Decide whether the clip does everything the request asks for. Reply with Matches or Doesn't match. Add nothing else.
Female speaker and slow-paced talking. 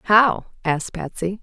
Matches